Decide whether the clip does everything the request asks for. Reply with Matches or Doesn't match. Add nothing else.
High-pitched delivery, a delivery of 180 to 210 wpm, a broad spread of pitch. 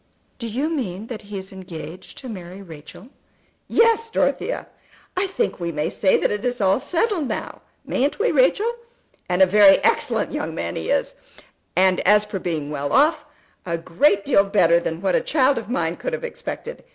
Matches